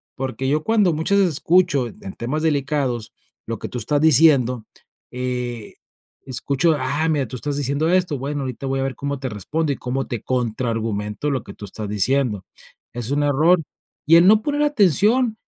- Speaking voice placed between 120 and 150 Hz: Yes, medium, 140 Hz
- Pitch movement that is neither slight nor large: Yes, average, 4.5 semitones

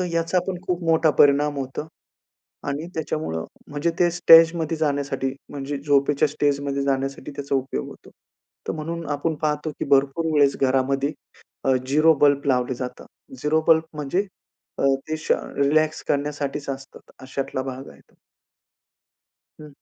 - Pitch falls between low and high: Yes, medium, 145 Hz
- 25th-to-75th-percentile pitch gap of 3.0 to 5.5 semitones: No, narrow, 2.4 semitones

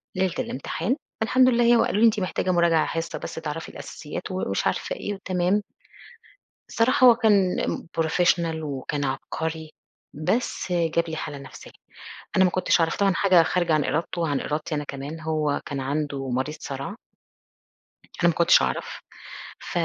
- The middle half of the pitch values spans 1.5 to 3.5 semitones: No, average, 4.0 semitones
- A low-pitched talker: No, medium, 165 Hz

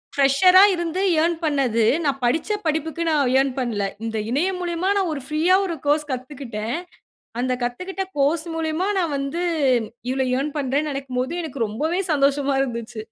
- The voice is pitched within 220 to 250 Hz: No, very high, 285 Hz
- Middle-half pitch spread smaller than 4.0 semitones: No, average, 4.3 semitones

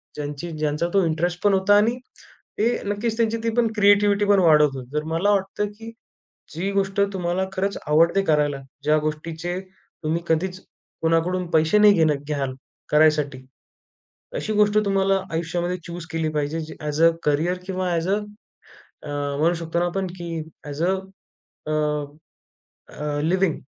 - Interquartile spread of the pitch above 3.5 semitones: Yes, average, 4.1 semitones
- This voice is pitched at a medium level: Yes, medium, 170 Hz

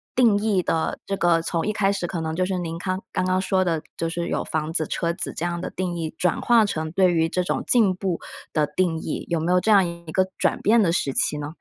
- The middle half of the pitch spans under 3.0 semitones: Yes, narrow, 2.5 semitones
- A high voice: No, medium, 175 Hz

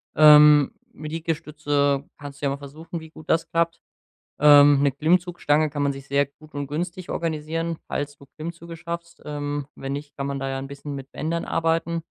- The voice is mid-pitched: Yes, medium, 150 Hz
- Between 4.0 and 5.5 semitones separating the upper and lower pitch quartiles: No, narrow, 2.6 semitones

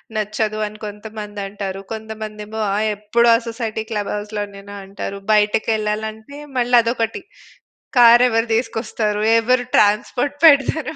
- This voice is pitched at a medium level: No, high, 220 Hz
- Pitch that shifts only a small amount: Yes, narrow, 1.8 semitones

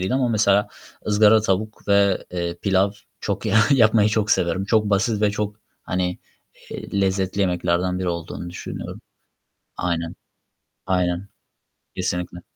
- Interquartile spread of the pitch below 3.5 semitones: Yes, average, 2.7 semitones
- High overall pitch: No, very low, 95 Hz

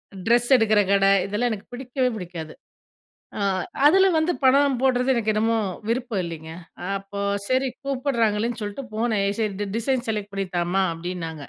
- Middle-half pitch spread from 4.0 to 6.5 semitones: Yes, average, 4.3 semitones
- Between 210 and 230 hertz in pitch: Yes, high, 220 Hz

